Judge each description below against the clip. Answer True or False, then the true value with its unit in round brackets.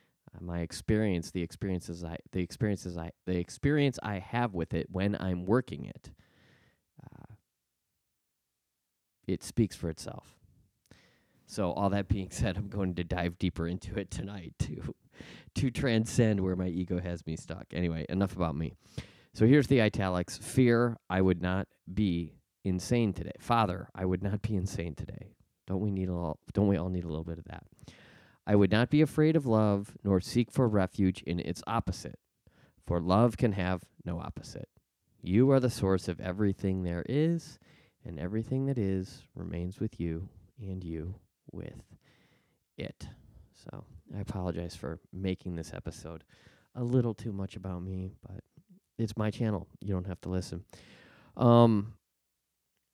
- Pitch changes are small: False (4.2 semitones)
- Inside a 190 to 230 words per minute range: False (160 wpm)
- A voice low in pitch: True (95 Hz)